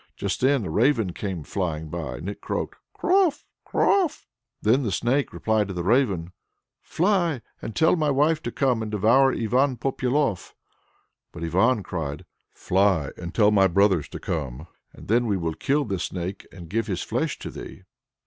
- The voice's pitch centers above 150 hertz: No, low, 105 Hz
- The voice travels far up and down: Yes, wide, 7.0 semitones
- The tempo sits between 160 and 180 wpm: Yes, average, 175 wpm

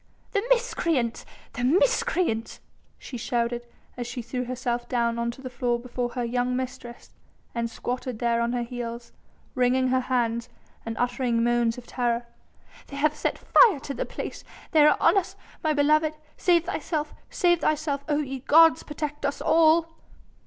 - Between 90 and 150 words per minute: No, average, 165 wpm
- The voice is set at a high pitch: Yes, very high, 255 Hz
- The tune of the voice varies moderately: Yes, average, 4.3 semitones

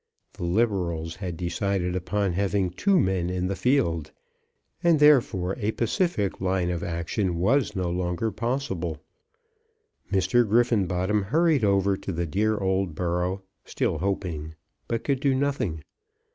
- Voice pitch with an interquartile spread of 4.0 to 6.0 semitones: Yes, average, 4.3 semitones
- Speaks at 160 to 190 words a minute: No, slow, 135 wpm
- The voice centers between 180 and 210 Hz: No, very low, 95 Hz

